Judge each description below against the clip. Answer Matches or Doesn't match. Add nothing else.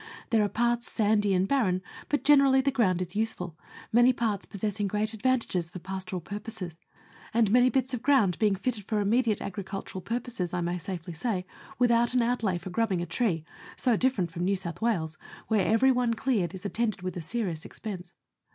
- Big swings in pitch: Doesn't match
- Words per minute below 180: Doesn't match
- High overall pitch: Matches